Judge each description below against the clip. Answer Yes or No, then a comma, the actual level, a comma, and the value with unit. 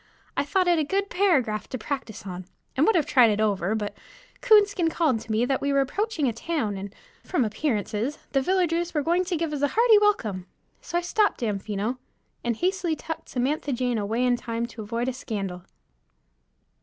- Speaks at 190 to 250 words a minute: Yes, average, 195 wpm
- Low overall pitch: No, very high, 265 Hz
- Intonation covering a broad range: Yes, wide, 7.7 semitones